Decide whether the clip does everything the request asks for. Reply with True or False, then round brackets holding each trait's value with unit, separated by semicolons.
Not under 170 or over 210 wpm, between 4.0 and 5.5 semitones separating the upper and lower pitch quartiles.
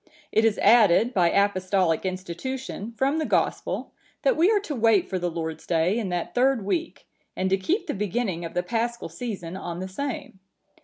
True (190 wpm; 5.2 semitones)